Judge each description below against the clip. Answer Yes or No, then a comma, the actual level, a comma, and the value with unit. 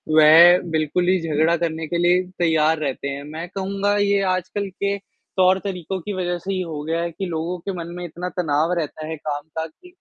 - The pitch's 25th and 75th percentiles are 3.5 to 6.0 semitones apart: No, average, 2.8 semitones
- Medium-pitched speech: Yes, medium, 170 Hz